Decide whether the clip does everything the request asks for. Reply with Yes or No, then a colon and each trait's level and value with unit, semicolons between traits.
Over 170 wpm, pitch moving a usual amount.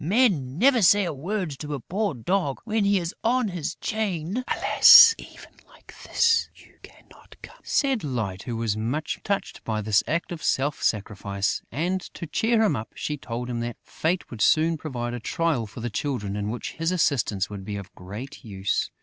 No: average, 190 wpm; wide, 8.8 semitones